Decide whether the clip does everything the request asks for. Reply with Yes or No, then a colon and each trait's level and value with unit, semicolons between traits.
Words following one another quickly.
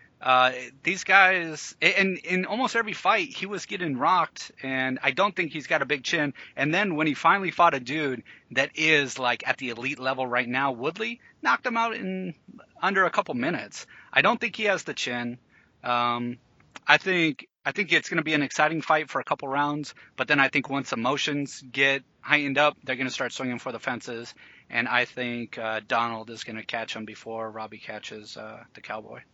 Yes: fast, 210 wpm